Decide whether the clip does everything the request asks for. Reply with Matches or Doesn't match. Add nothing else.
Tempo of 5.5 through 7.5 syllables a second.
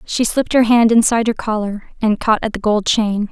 Matches